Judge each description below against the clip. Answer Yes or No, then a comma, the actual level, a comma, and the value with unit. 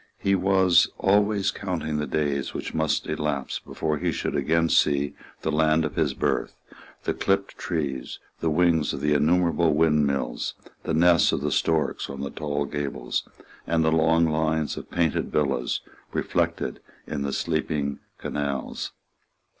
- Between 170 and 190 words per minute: No, average, 150 wpm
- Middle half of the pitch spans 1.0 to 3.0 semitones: Yes, narrow, 2.4 semitones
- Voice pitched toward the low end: Yes, very low, 80 Hz